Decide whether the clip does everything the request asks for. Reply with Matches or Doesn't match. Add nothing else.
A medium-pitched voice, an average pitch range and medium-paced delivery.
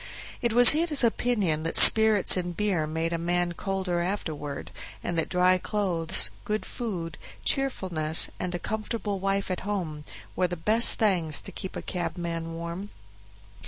Matches